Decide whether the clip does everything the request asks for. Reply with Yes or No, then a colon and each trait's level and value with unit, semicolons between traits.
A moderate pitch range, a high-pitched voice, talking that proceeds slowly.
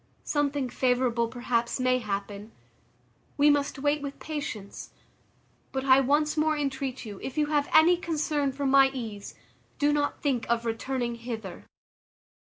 No: average, 3.6 semitones; very high, 265 Hz; average, 145 wpm